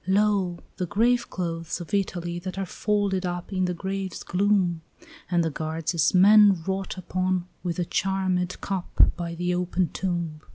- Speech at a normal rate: Yes, average, 160 wpm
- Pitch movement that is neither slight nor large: No, narrow, 2.0 semitones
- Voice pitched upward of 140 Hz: Yes, medium, 185 Hz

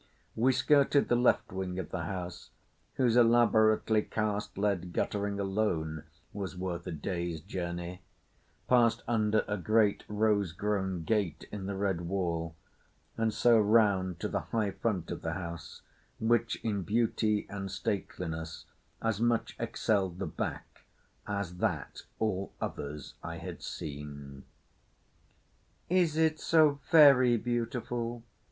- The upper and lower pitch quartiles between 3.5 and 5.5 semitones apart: Yes, average, 4.3 semitones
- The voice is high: No, low, 100 Hz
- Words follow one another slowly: Yes, slow, 130 wpm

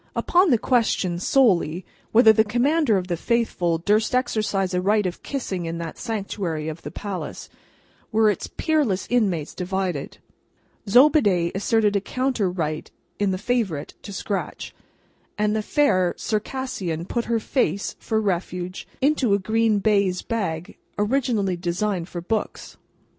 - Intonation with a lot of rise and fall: No, average, 4.1 semitones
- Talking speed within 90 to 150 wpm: Yes, average, 140 wpm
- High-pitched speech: Yes, high, 205 Hz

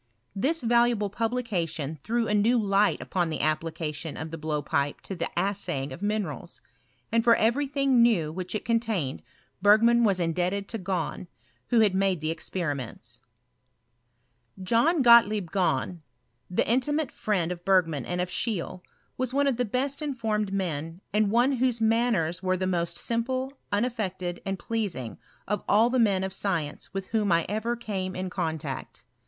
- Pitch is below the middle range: No, high, 200 Hz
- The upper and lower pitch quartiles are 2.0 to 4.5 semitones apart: No, average, 5.2 semitones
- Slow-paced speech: No, average, 160 wpm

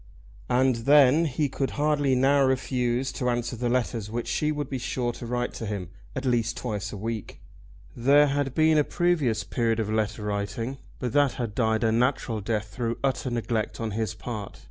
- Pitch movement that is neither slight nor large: Yes, average, 3.3 semitones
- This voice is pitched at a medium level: No, low, 120 Hz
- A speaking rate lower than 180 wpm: No, average, 190 wpm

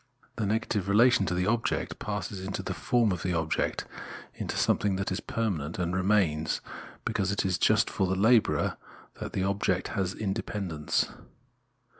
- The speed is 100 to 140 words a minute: No, average, 165 wpm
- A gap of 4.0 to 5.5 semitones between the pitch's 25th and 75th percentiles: No, narrow, 2.6 semitones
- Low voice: Yes, very low, 95 Hz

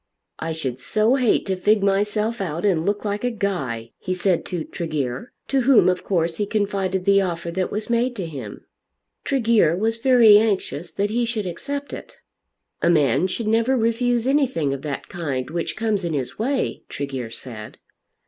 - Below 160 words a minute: No, average, 180 wpm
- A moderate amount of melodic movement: No, wide, 5.7 semitones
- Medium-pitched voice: No, high, 195 Hz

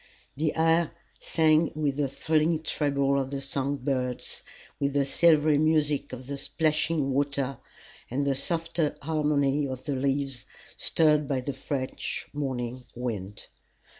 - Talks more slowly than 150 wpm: Yes, slow, 135 wpm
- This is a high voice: No, medium, 140 Hz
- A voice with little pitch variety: Yes, narrow, 2.3 semitones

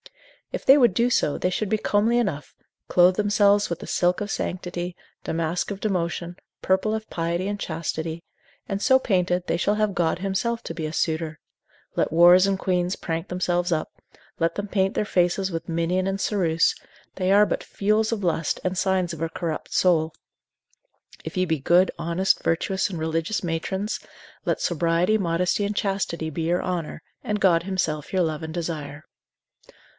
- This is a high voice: No, medium, 180 Hz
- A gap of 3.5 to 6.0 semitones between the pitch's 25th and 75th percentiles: No, average, 3.0 semitones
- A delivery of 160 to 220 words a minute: Yes, average, 180 wpm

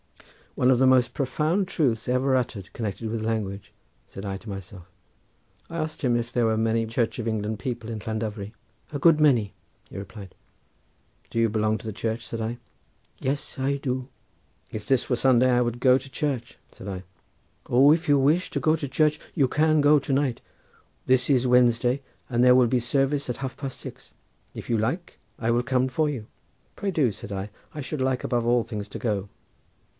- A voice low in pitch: Yes, low, 125 Hz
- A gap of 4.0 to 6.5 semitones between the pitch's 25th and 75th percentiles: No, average, 3.5 semitones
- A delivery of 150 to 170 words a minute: No, average, 200 wpm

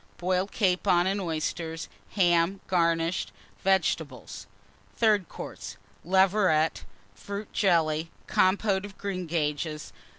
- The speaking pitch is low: No, medium, 180 Hz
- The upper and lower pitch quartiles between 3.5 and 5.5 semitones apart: No, average, 2.8 semitones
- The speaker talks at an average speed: No, slow, 90 wpm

